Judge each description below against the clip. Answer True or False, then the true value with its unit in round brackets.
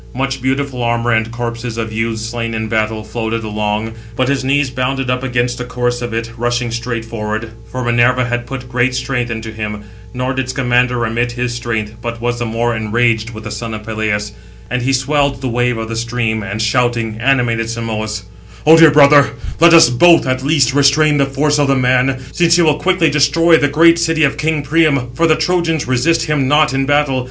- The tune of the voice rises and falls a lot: False (3.3 semitones)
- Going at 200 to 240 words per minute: True (205 wpm)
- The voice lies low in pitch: True (125 Hz)